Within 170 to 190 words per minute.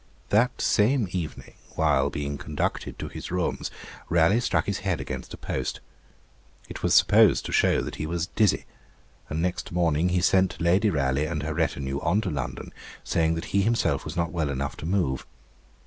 Yes: average, 180 wpm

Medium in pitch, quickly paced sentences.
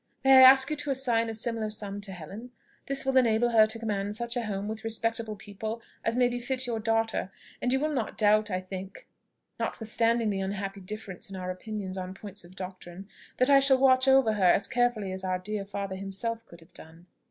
No: high, 215 Hz; fast, 215 wpm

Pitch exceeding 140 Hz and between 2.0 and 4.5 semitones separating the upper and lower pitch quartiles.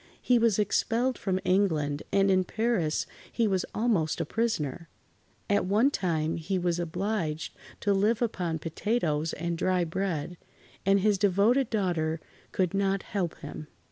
Yes: high, 190 Hz; average, 4.2 semitones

